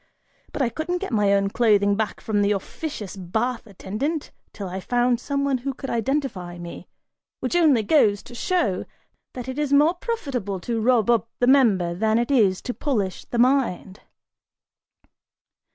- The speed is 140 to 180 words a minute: Yes, average, 170 wpm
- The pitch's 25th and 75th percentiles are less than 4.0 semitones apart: No, wide, 5.5 semitones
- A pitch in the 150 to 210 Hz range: No, high, 235 Hz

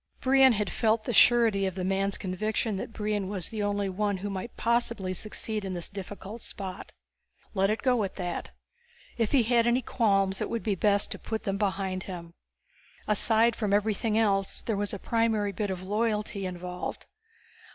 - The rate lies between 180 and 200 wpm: Yes, average, 185 wpm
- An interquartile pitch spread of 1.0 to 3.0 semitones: Yes, narrow, 2.5 semitones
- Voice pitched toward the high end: Yes, high, 205 Hz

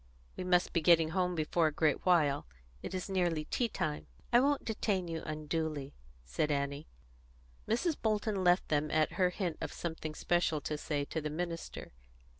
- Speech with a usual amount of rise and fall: Yes, average, 3.2 semitones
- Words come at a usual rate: Yes, average, 175 wpm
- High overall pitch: No, medium, 165 Hz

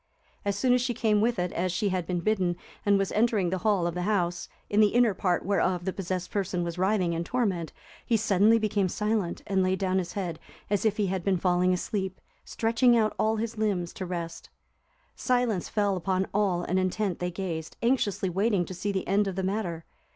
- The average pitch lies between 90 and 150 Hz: No, high, 195 Hz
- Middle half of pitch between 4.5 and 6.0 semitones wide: No, average, 3.0 semitones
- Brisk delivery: Yes, fast, 215 wpm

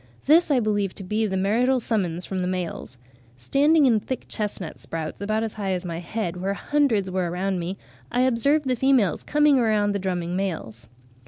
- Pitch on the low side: No, high, 200 Hz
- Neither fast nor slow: Yes, average, 190 wpm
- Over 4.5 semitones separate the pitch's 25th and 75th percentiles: Yes, average, 5.3 semitones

